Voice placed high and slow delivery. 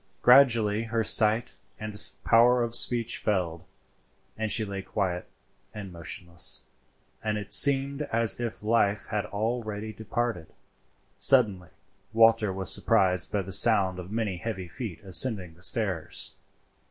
No: low, 105 Hz; slow, 130 wpm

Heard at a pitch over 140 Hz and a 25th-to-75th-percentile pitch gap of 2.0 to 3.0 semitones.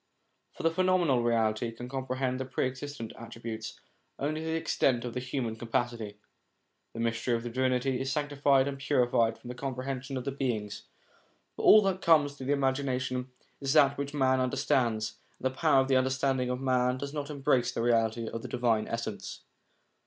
No: low, 130 Hz; average, 2.7 semitones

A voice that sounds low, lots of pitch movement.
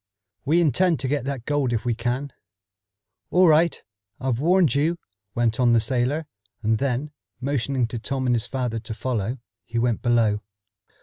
No: low, 125 Hz; average, 3.5 semitones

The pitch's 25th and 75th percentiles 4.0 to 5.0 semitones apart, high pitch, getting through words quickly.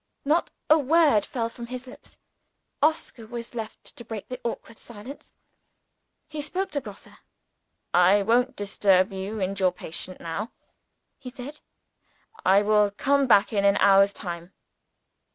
No: average, 4.5 semitones; high, 225 Hz; average, 145 wpm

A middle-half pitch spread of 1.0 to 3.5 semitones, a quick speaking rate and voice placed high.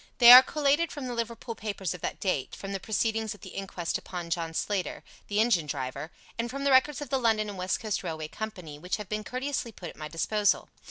No: average, 5.2 semitones; fast, 230 wpm; high, 210 Hz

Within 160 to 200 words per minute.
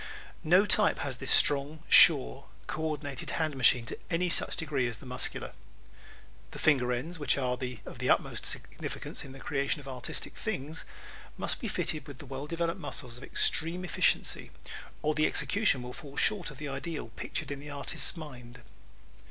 Yes: average, 175 wpm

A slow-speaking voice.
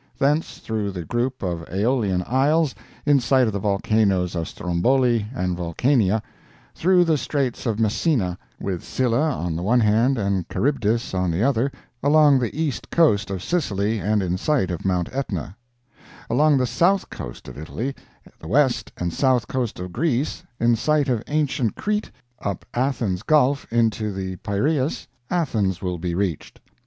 No: average, 160 wpm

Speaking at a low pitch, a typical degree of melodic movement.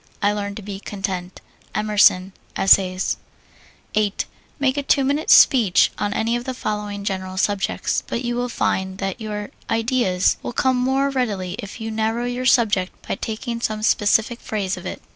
No: high, 215 Hz; average, 3.7 semitones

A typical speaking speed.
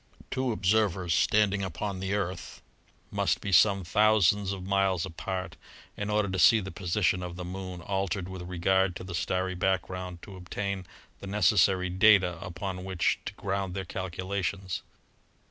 Yes: average, 155 wpm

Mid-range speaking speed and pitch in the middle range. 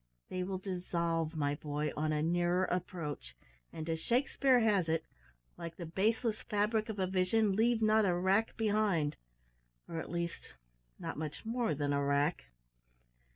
Yes: average, 155 wpm; medium, 180 Hz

